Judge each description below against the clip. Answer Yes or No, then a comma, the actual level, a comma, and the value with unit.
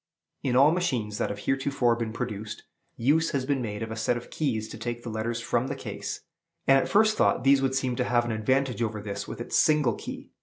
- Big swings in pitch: No, average, 3.4 semitones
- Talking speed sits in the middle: No, fast, 235 wpm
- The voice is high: No, low, 120 Hz